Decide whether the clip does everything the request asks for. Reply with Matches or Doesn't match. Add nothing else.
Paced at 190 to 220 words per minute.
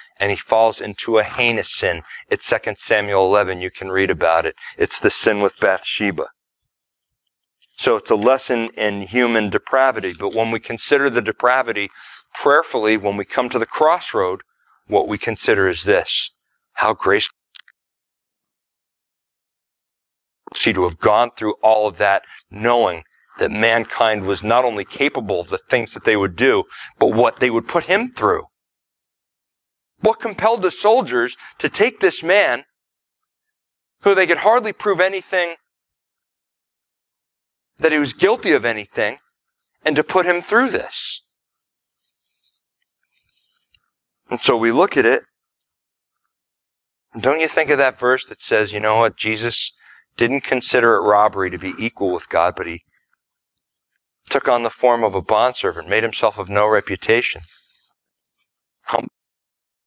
Doesn't match